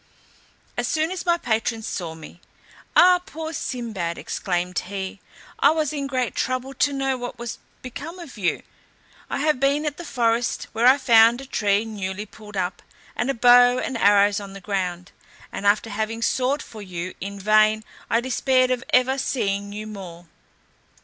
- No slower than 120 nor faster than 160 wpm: No, average, 175 wpm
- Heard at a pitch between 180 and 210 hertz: No, high, 230 Hz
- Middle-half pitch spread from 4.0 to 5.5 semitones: Yes, average, 4.8 semitones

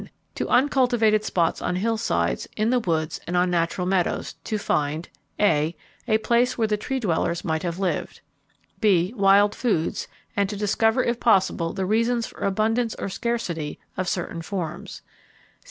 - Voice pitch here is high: Yes, high, 200 Hz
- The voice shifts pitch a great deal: No, average, 4.6 semitones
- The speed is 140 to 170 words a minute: Yes, average, 155 wpm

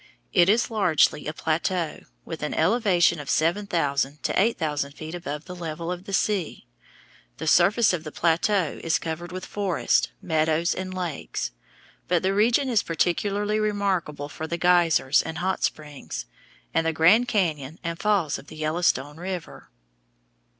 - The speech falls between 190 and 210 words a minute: No, average, 160 wpm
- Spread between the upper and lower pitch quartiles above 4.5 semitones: No, average, 3.8 semitones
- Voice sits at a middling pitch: Yes, medium, 170 Hz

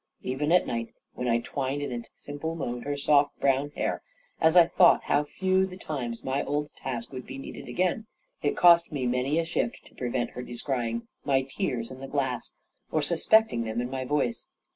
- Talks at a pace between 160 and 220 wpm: Yes, average, 200 wpm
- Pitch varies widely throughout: No, average, 3.8 semitones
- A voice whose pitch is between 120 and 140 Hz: Yes, low, 135 Hz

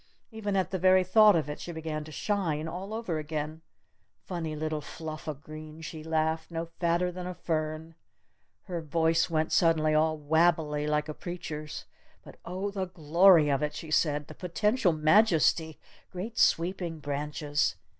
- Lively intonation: No, average, 2.7 semitones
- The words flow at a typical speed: Yes, average, 165 wpm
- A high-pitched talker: No, medium, 160 Hz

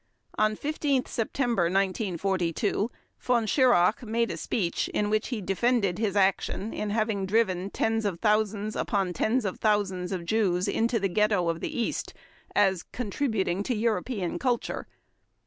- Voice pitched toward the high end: Yes, high, 210 Hz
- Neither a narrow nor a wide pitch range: Yes, average, 3.2 semitones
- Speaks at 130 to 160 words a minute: Yes, average, 145 wpm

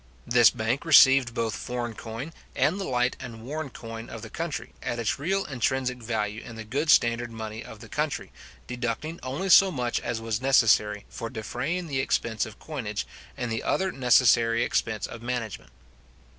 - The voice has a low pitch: Yes, low, 120 Hz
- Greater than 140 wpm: Yes, average, 175 wpm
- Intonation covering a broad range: No, average, 3.0 semitones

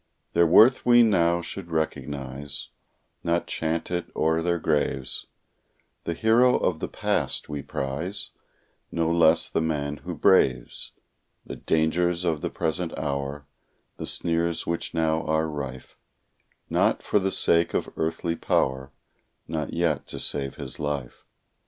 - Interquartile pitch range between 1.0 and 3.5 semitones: Yes, average, 2.9 semitones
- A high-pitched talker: No, very low, 80 Hz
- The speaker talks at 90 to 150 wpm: Yes, average, 140 wpm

